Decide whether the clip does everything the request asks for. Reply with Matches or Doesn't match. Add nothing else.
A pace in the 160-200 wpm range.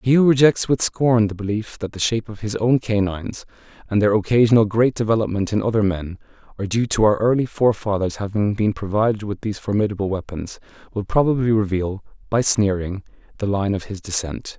Matches